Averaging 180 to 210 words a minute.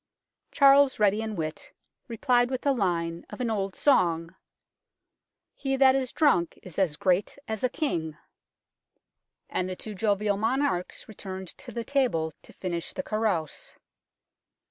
No: average, 145 wpm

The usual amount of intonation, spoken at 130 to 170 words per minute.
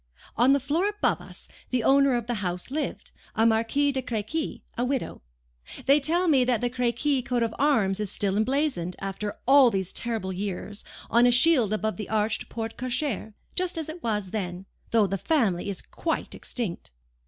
No: average, 5.0 semitones; average, 185 wpm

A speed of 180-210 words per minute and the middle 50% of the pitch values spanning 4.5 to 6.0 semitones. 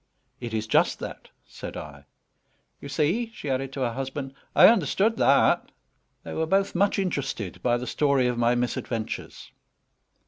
No: average, 160 wpm; average, 5.1 semitones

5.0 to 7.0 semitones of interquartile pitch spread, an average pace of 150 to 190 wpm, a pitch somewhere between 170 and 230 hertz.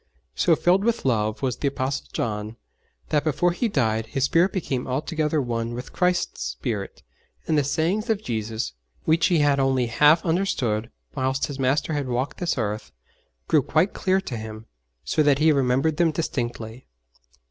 No: average, 5.3 semitones; average, 170 wpm; medium, 140 Hz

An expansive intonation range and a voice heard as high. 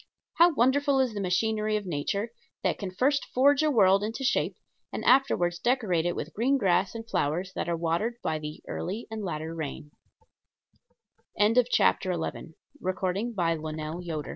Yes: wide, 5.8 semitones; high, 195 Hz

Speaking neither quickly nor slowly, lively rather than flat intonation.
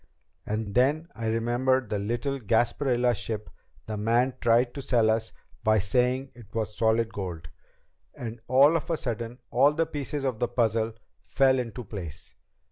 No: average, 160 wpm; average, 2.9 semitones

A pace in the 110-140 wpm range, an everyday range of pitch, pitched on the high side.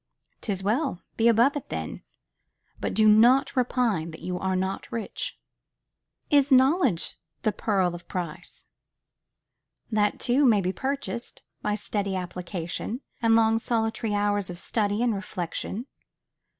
Yes: slow, 135 wpm; average, 4.2 semitones; high, 210 Hz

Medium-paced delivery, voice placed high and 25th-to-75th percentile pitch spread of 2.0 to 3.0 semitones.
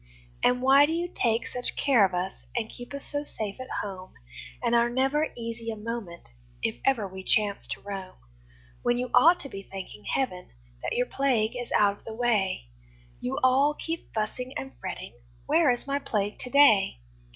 No: average, 190 wpm; high, 235 Hz; average, 5.0 semitones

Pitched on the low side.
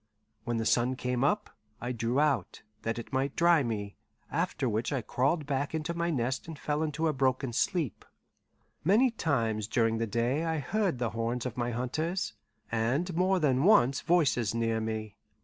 Yes: low, 130 Hz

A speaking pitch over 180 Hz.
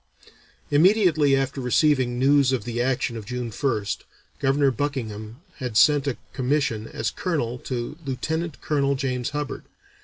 No: low, 135 Hz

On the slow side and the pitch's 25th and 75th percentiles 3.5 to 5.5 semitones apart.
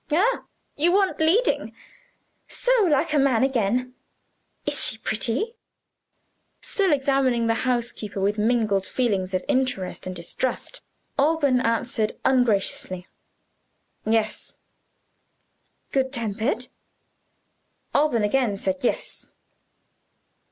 Yes: slow, 95 wpm; average, 4.5 semitones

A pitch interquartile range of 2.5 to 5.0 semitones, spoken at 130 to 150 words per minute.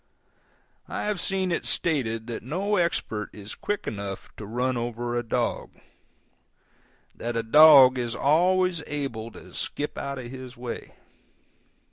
No: wide, 5.6 semitones; average, 140 wpm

